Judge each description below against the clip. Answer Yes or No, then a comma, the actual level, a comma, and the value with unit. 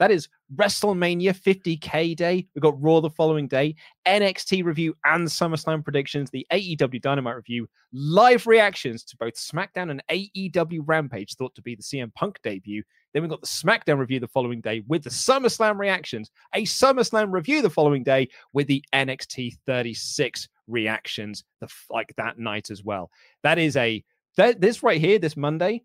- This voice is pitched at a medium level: Yes, medium, 150 Hz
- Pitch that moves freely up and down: Yes, wide, 6.5 semitones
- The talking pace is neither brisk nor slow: Yes, average, 165 wpm